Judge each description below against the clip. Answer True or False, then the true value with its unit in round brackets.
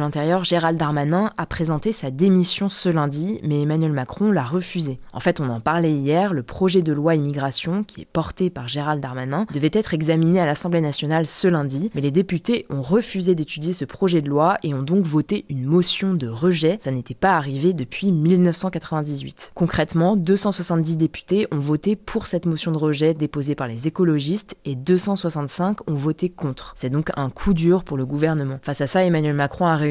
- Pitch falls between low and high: True (165 Hz)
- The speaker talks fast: False (195 wpm)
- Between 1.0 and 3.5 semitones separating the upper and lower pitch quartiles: False (3.9 semitones)